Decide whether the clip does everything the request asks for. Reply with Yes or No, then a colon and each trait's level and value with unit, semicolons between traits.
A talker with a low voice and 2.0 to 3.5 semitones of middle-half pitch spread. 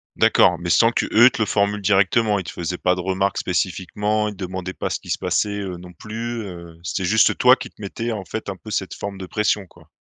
Yes: low, 100 Hz; average, 2.8 semitones